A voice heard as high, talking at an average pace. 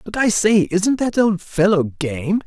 Yes: high, 195 Hz; average, 195 wpm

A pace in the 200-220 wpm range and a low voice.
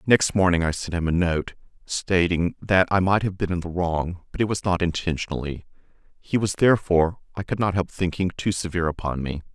Yes: fast, 205 wpm; very low, 90 Hz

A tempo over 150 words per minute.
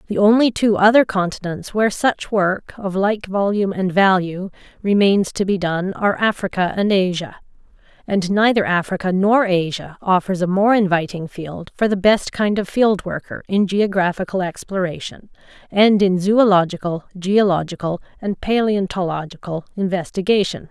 No: average, 140 wpm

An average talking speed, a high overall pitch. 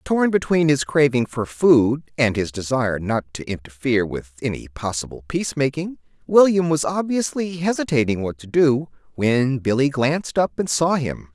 No: average, 165 wpm; low, 135 Hz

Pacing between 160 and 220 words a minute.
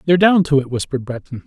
No: fast, 245 wpm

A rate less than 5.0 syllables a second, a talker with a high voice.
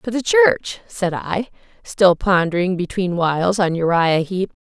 No: 4.1 syllables/s; medium, 180 Hz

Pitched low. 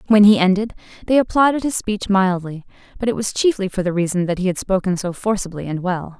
No: high, 195 Hz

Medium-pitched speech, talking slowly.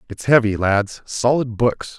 No: low, 115 Hz; slow, 120 wpm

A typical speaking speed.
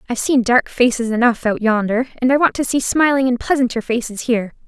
No: fast, 220 wpm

